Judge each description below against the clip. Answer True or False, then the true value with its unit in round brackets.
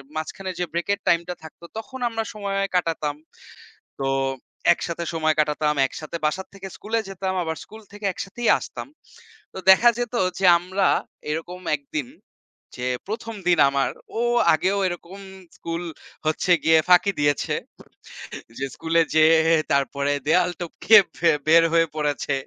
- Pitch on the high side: False (170 Hz)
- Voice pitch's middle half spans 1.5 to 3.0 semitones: False (3.7 semitones)